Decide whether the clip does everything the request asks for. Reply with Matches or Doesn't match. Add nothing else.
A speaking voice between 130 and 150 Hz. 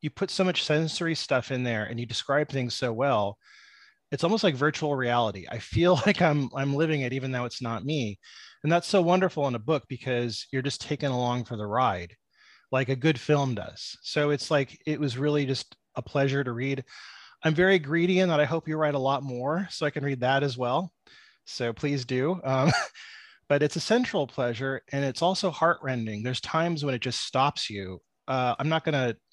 Matches